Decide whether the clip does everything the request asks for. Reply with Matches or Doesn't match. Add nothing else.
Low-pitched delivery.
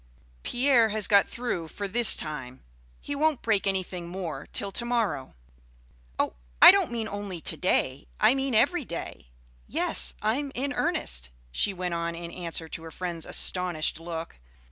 Doesn't match